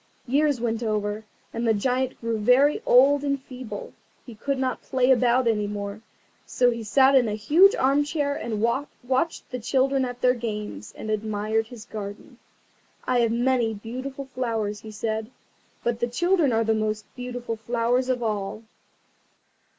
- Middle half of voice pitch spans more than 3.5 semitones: No, average, 3.2 semitones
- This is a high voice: Yes, high, 240 Hz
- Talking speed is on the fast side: No, average, 160 wpm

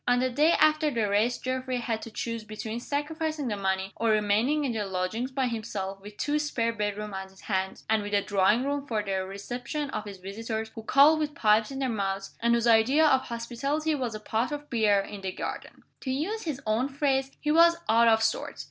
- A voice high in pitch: Yes, high, 230 Hz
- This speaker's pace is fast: Yes, fast, 220 wpm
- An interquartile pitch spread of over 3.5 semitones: Yes, average, 4.9 semitones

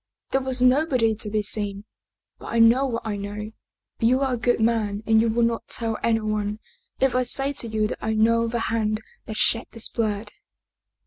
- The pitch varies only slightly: Yes, narrow, 2.0 semitones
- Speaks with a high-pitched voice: Yes, high, 225 Hz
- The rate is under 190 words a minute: No, average, 200 wpm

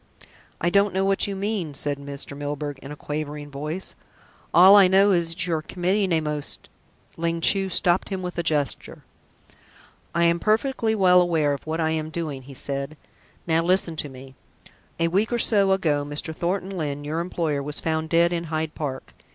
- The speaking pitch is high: No, medium, 165 Hz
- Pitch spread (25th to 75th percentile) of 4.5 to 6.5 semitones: No, average, 4.0 semitones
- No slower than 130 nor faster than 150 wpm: No, average, 195 wpm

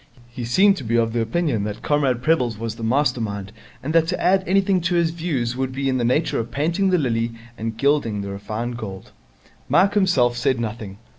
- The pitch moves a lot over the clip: Yes, wide, 6.2 semitones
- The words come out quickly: Yes, fast, 215 wpm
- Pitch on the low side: Yes, low, 125 Hz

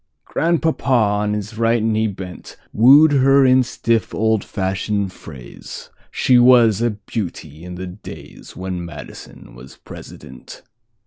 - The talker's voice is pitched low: Yes, low, 110 Hz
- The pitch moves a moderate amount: Yes, average, 4.6 semitones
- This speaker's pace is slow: Yes, slow, 115 wpm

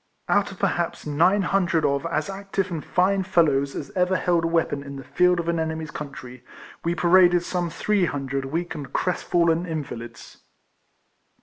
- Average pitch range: Yes, average, 3.6 semitones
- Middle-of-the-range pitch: Yes, medium, 170 Hz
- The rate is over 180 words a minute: No, average, 175 wpm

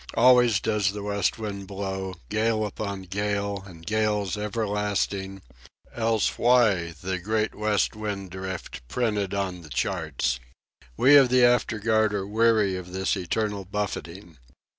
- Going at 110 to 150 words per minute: Yes, slow, 135 wpm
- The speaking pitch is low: Yes, low, 100 Hz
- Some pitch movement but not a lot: No, narrow, 2.2 semitones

